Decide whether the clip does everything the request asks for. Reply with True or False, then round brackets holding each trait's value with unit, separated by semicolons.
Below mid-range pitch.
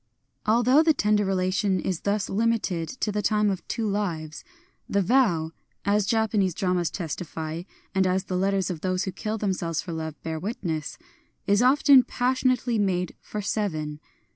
False (195 Hz)